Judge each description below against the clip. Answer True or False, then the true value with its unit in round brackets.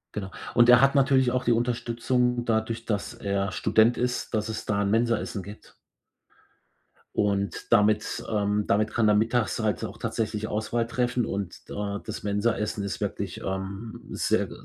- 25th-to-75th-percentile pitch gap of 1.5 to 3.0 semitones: True (2.6 semitones)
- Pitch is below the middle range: True (110 Hz)